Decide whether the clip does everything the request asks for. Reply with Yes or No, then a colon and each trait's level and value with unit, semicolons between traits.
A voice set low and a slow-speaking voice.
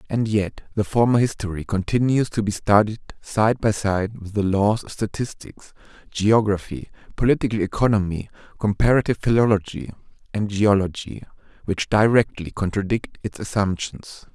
Yes: low, 105 Hz; slow, 120 wpm